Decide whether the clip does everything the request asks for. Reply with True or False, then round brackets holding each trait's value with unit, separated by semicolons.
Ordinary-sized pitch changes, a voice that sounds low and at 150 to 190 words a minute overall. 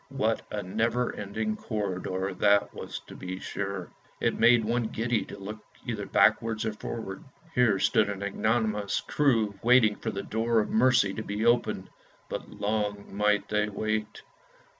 False (2.0 semitones; 110 Hz; 160 wpm)